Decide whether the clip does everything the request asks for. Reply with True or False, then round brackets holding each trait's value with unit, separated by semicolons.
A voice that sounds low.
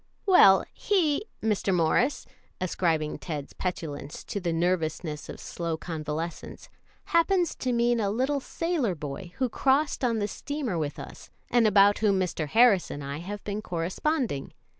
False (195 Hz)